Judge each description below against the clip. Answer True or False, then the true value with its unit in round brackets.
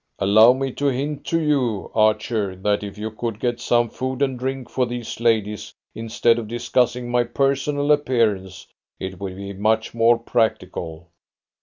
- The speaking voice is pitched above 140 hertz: False (115 Hz)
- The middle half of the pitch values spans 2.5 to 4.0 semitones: True (3.5 semitones)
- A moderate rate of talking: True (160 wpm)